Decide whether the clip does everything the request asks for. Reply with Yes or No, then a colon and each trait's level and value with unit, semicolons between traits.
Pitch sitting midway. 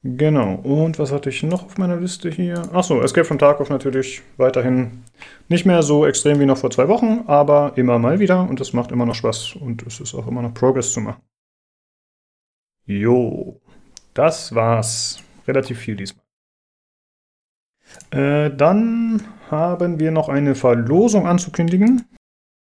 Yes: medium, 145 Hz